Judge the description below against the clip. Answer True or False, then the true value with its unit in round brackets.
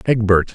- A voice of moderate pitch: False (105 Hz)